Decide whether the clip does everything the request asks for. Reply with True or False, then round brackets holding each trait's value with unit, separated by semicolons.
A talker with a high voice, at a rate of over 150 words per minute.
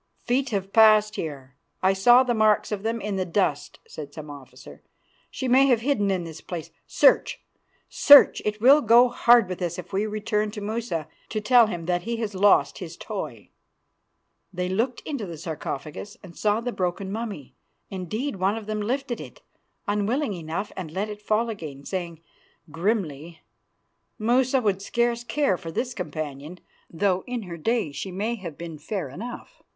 True (205 Hz; 175 wpm)